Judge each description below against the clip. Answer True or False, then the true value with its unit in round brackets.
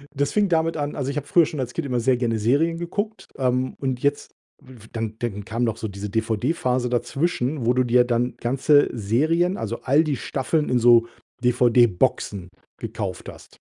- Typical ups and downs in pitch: True (3.8 semitones)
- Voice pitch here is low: True (125 Hz)